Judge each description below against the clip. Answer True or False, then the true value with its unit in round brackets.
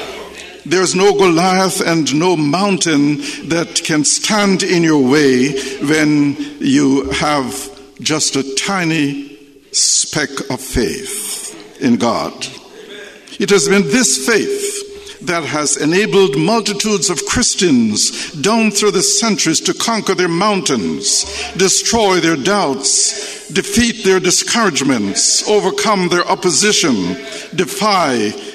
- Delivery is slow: True (110 wpm)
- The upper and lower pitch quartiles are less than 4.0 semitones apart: False (5.3 semitones)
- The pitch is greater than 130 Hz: True (190 Hz)